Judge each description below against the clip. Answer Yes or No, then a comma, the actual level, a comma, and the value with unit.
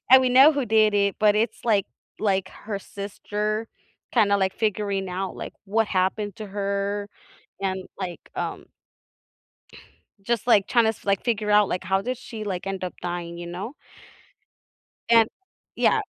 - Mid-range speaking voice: No, high, 205 Hz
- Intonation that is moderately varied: No, narrow, 2.3 semitones